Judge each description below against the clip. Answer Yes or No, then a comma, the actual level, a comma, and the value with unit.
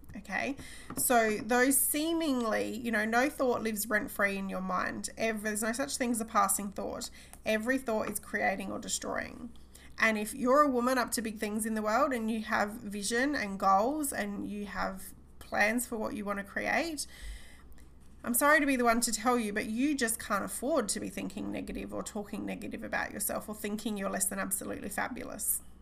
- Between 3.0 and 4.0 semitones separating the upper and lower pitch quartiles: Yes, average, 3.4 semitones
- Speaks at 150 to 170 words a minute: No, average, 200 wpm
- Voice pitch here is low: No, high, 225 Hz